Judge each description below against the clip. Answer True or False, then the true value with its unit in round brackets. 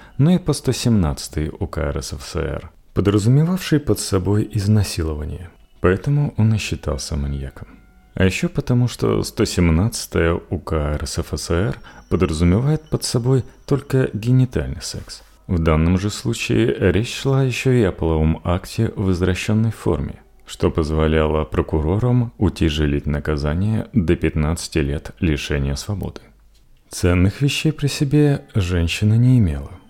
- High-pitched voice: False (95 Hz)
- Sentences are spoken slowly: False (120 wpm)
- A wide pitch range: True (6.9 semitones)